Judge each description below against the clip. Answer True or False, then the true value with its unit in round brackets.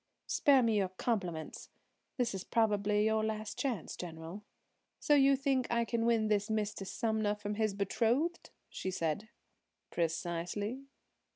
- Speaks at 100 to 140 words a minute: True (135 wpm)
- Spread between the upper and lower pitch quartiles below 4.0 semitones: True (3.3 semitones)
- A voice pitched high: True (215 Hz)